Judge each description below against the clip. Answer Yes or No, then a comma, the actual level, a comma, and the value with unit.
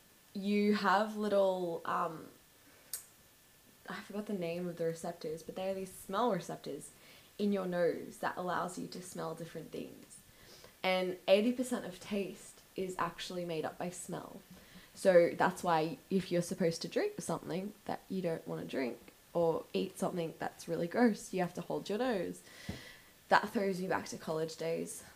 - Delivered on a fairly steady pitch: No, average, 3.1 semitones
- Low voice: No, medium, 185 Hz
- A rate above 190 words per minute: No, average, 170 wpm